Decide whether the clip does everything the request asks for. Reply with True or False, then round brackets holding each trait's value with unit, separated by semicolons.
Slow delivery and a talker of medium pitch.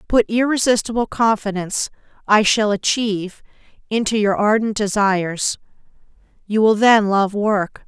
False (115 wpm; 210 Hz)